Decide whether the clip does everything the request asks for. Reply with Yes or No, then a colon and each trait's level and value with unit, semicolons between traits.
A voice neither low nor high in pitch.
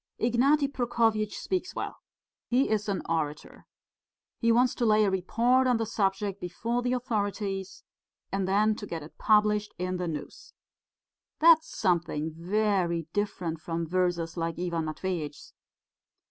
No: high, 200 Hz